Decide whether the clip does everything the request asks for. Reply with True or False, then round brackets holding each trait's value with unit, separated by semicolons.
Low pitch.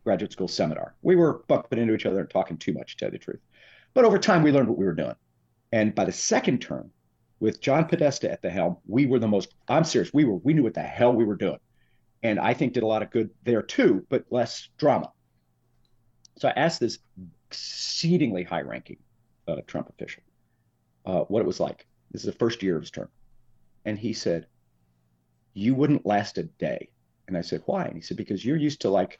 True (110 Hz)